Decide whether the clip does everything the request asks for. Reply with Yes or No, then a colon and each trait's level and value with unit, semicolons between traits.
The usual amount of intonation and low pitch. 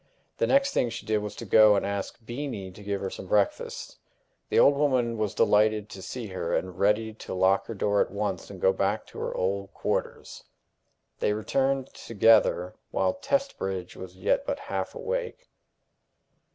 Yes: average, 4.5 semitones; low, 105 Hz